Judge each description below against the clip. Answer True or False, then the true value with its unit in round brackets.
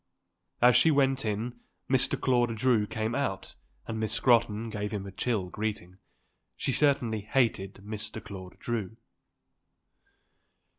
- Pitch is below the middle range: True (110 Hz)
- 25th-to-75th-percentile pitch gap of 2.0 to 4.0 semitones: True (2.9 semitones)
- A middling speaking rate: False (130 wpm)